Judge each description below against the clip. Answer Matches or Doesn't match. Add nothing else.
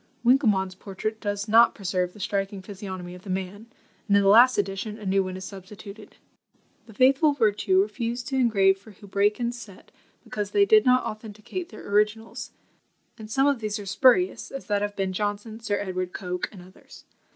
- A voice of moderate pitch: Doesn't match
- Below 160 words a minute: Doesn't match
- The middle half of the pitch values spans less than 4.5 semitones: Matches